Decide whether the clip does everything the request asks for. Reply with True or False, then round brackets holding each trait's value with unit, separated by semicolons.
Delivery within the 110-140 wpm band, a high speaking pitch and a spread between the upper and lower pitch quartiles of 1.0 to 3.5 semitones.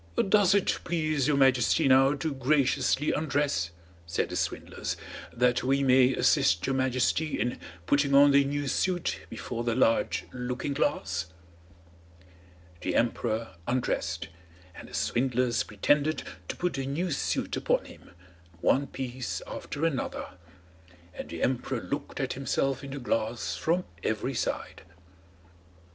False (135 wpm; 135 Hz; 2.9 semitones)